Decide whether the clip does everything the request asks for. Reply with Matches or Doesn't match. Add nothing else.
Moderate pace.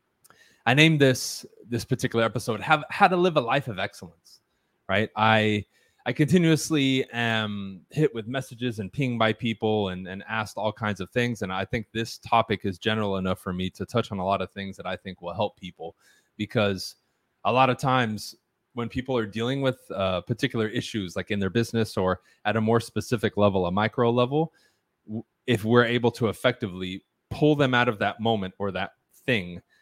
Matches